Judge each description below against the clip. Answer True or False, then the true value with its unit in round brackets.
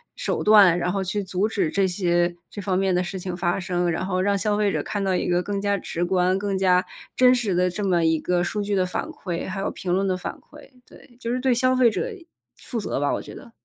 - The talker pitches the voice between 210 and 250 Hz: False (190 Hz)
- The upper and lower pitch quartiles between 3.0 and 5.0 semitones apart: False (2.6 semitones)